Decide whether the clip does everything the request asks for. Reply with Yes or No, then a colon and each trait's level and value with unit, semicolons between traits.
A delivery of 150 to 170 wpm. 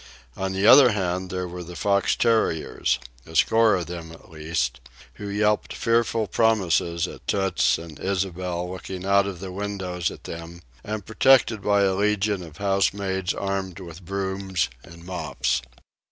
Yes: average, 155 wpm